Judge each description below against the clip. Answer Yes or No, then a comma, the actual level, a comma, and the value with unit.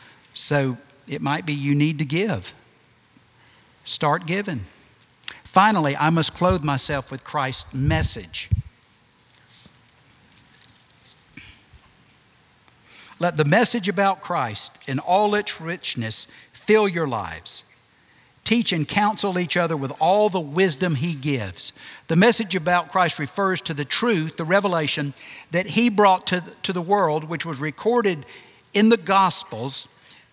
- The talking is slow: Yes, slow, 125 wpm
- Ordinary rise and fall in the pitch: No, wide, 6.5 semitones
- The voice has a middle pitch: Yes, medium, 155 Hz